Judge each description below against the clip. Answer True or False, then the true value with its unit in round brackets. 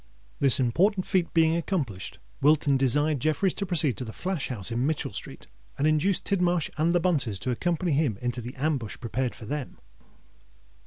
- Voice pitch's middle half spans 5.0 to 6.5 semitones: True (5.4 semitones)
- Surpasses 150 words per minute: True (175 wpm)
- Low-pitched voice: False (150 Hz)